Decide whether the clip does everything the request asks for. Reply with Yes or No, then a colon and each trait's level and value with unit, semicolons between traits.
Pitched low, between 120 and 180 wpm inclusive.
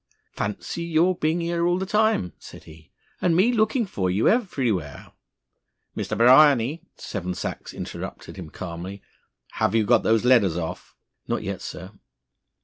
Yes: low, 125 Hz; average, 150 wpm